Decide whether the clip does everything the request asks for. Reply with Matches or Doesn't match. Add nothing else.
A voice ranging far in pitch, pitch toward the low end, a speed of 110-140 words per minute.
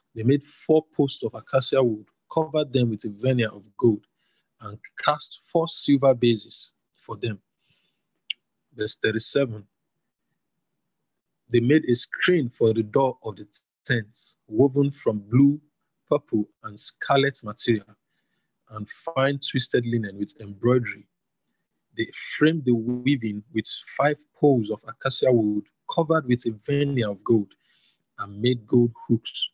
Doesn't match